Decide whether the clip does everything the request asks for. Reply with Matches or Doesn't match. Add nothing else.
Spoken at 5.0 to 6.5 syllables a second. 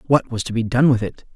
Matches